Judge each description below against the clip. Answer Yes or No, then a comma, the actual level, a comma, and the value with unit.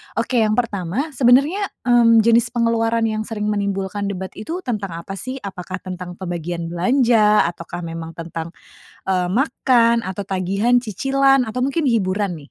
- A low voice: No, high, 210 Hz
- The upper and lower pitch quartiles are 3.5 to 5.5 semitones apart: Yes, average, 4.8 semitones